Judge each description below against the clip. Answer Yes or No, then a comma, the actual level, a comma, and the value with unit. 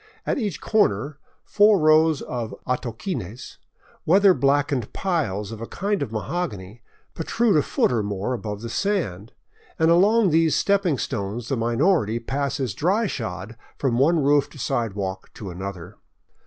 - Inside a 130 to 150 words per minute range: Yes, average, 140 wpm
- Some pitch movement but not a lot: No, wide, 7.7 semitones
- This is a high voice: No, low, 135 Hz